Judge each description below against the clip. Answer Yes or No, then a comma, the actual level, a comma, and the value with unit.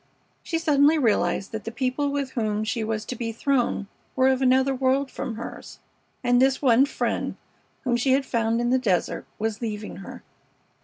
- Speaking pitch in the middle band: No, very high, 250 Hz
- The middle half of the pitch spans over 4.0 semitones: No, average, 3.2 semitones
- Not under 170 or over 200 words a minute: Yes, average, 185 wpm